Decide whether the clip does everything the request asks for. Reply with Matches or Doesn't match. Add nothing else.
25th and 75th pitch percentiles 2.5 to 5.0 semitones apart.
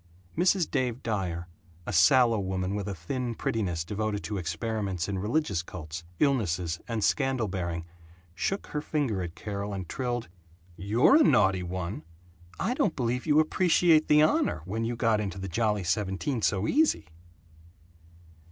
Doesn't match